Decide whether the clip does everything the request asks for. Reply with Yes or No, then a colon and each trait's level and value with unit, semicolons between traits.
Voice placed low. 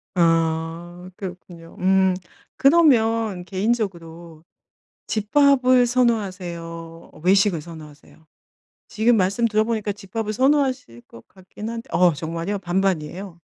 No: high, 190 Hz